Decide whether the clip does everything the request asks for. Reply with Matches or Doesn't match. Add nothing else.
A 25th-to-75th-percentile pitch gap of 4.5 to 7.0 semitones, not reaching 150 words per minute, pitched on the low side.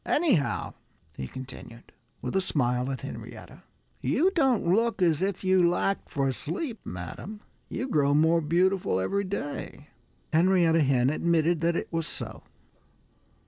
Doesn't match